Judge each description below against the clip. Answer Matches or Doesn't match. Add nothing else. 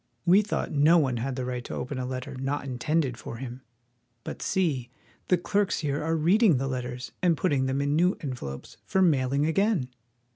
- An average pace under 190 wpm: Doesn't match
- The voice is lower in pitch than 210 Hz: Matches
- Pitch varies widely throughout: Doesn't match